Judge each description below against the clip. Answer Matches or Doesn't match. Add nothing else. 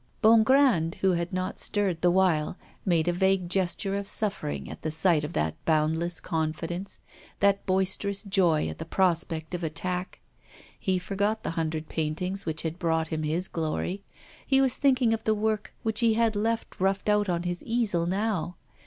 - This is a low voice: Doesn't match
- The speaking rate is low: Doesn't match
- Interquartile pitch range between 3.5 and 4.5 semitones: Matches